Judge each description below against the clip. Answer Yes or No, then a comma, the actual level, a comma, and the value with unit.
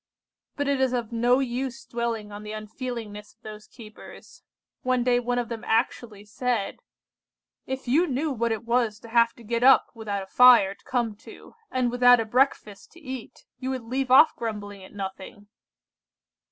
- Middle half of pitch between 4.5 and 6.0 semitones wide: No, average, 2.9 semitones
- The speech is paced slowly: No, average, 180 wpm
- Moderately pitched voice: No, high, 235 Hz